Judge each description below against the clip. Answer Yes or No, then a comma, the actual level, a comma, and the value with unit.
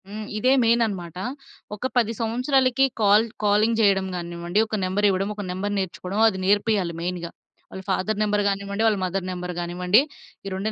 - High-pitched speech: Yes, high, 200 Hz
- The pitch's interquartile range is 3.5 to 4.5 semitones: No, average, 2.9 semitones